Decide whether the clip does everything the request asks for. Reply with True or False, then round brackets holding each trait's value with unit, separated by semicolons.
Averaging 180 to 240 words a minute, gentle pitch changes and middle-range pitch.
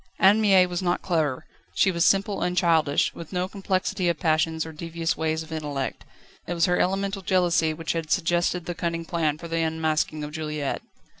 True (190 wpm; 2.3 semitones; 170 Hz)